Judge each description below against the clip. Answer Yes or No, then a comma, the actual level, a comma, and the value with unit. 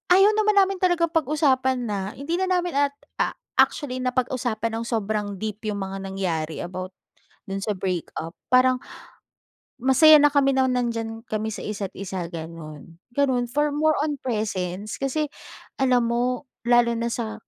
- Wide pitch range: Yes, wide, 5.8 semitones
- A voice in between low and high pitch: No, high, 240 Hz